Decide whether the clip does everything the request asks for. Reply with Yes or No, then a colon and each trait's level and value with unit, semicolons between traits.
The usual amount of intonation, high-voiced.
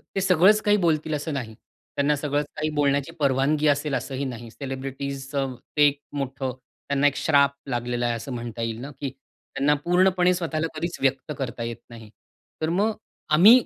No: average, 3.1 semitones; medium, 140 Hz